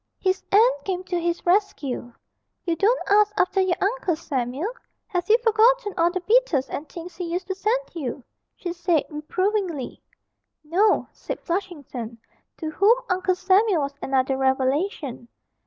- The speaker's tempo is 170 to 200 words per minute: No, average, 150 wpm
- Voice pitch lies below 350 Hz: No, very high, 360 Hz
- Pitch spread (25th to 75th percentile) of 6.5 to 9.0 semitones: No, average, 5.2 semitones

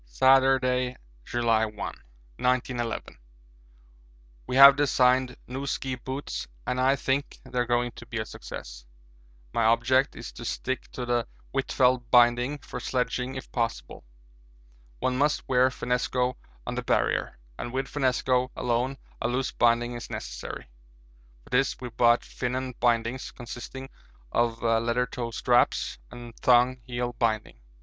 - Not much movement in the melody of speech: Yes, narrow, 1.7 semitones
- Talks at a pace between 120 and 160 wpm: Yes, average, 140 wpm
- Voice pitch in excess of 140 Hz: No, low, 125 Hz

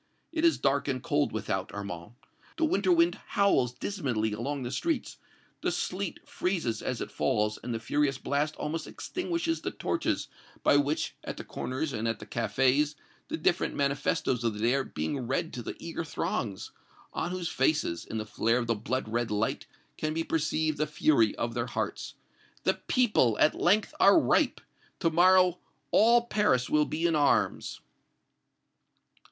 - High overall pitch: No, medium, 145 Hz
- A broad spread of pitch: Yes, wide, 6.4 semitones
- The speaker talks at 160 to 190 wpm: Yes, average, 170 wpm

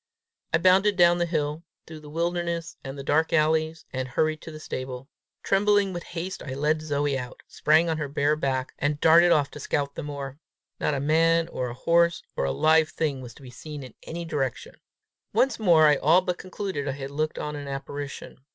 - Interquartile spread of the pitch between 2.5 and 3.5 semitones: Yes, average, 3.1 semitones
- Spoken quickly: Yes, fast, 210 wpm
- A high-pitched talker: No, medium, 155 Hz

